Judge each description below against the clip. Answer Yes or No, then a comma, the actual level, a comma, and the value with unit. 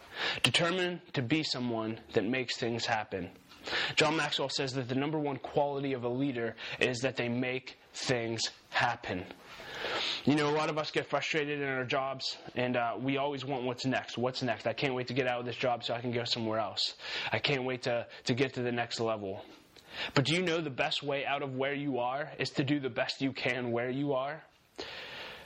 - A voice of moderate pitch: No, low, 130 Hz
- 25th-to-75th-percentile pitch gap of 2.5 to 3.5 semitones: Yes, average, 2.9 semitones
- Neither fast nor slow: No, fast, 215 wpm